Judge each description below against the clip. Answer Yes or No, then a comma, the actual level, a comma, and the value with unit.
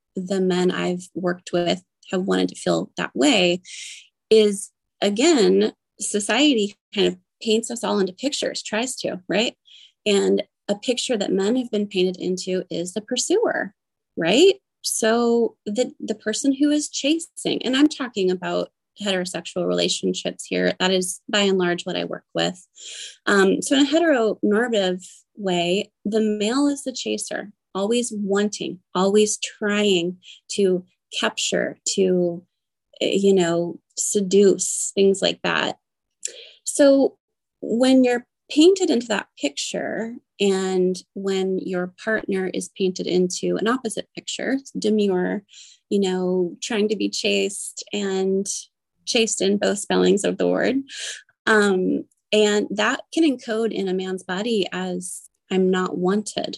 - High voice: Yes, high, 200 Hz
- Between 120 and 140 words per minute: Yes, slow, 135 wpm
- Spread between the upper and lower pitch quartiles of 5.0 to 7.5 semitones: No, average, 3.6 semitones